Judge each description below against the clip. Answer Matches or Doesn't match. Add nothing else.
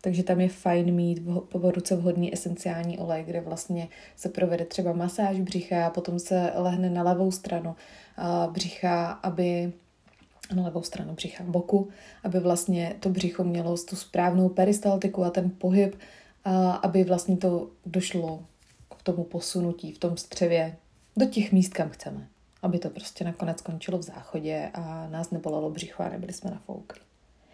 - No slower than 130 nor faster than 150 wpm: Doesn't match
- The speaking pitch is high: Doesn't match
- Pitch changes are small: Matches